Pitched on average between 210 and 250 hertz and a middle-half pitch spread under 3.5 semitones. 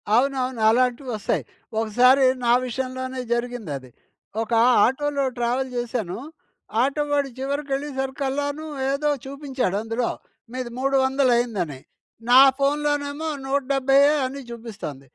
No: very high, 260 Hz; average, 2.7 semitones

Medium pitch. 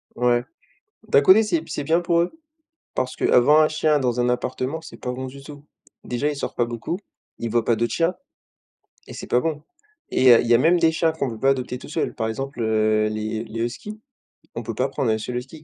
No: low, 130 Hz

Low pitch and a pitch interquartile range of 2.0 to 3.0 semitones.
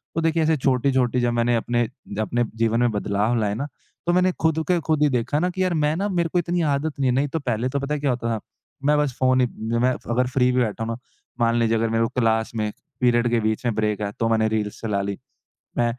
No: low, 120 Hz; average, 4.2 semitones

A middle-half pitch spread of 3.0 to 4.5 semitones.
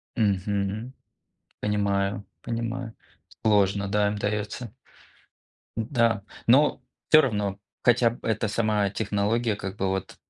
No: narrow, 2.5 semitones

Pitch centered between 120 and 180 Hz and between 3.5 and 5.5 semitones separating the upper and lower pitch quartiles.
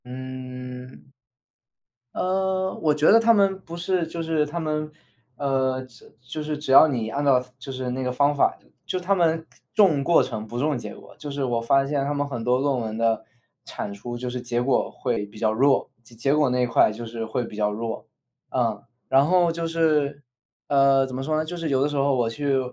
Yes: low, 135 Hz; average, 3.9 semitones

